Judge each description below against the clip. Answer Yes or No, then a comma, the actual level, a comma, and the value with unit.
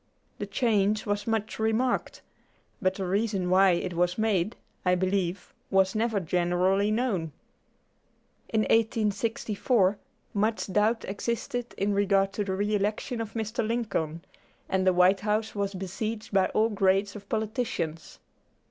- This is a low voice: No, high, 205 Hz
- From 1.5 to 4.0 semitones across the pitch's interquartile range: Yes, average, 2.7 semitones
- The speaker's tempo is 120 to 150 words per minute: Yes, average, 140 wpm